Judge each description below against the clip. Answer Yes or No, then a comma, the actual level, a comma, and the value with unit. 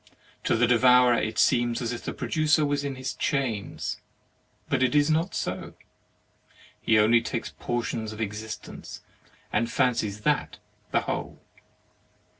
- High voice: No, low, 120 Hz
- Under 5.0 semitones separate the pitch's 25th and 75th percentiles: Yes, average, 3.6 semitones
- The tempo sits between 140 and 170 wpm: Yes, average, 145 wpm